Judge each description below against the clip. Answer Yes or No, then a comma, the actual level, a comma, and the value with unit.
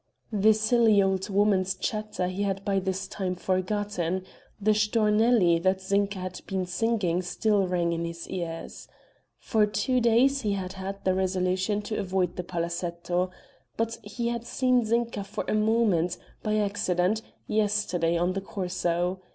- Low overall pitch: No, high, 195 Hz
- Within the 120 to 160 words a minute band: Yes, average, 150 wpm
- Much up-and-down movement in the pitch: No, average, 2.7 semitones